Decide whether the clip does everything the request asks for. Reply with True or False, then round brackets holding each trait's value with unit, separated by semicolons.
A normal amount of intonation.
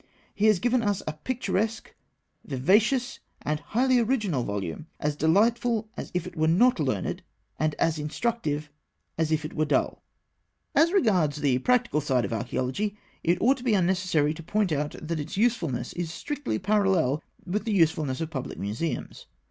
False (6.6 semitones)